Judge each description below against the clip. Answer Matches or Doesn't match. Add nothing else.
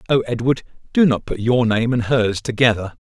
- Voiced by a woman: Doesn't match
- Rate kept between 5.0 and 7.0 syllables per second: Matches